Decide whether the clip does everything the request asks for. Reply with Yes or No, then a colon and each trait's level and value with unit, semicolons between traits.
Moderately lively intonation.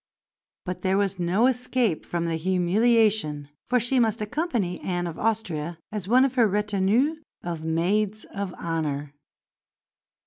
Yes: average, 4.7 semitones